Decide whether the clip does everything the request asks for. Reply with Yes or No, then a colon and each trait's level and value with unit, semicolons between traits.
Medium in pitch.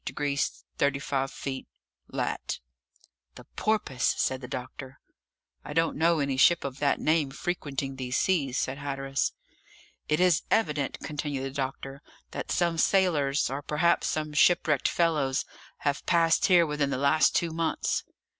Yes: medium, 145 Hz